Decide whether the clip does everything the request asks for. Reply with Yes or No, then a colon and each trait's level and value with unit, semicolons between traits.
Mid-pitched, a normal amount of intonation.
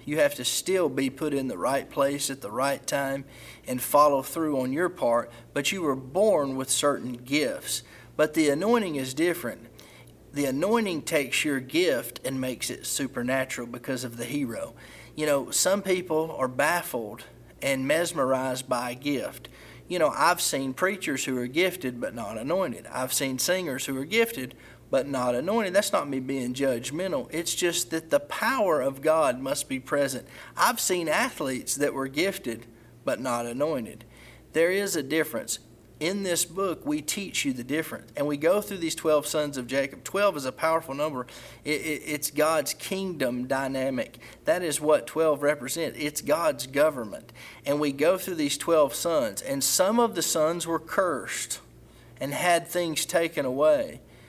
Yes: medium, 145 Hz; average, 4.0 semitones